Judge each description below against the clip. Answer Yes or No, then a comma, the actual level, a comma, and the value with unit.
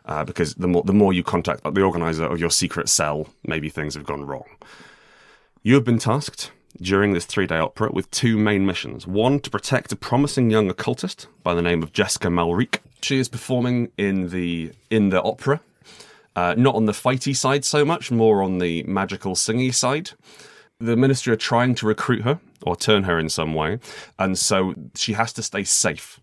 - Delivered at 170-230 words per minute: Yes, average, 195 wpm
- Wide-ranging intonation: Yes, wide, 6.1 semitones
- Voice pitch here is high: No, low, 105 Hz